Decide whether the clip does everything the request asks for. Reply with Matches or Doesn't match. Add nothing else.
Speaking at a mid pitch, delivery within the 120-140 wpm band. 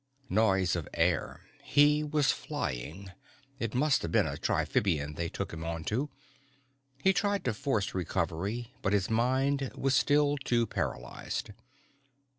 Doesn't match